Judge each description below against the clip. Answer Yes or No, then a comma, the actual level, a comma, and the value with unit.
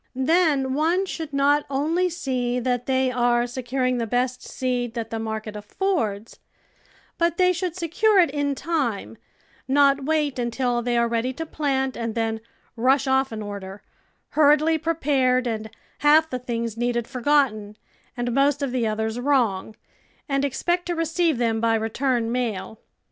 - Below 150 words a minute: No, average, 165 wpm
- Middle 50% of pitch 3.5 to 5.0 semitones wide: Yes, average, 4.1 semitones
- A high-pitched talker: Yes, very high, 255 Hz